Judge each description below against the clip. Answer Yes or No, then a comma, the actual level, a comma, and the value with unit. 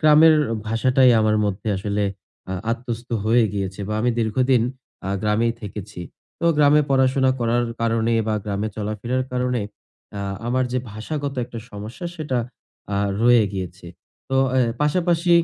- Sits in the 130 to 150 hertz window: No, low, 115 Hz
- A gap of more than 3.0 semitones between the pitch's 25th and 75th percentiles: Yes, average, 3.6 semitones